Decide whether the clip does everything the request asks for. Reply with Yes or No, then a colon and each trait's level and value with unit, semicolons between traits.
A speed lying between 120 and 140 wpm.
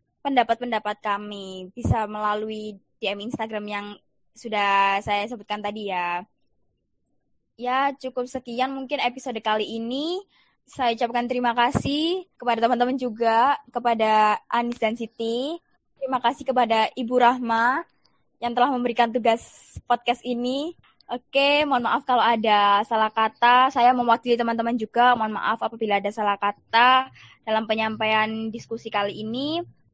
Yes: average, 125 wpm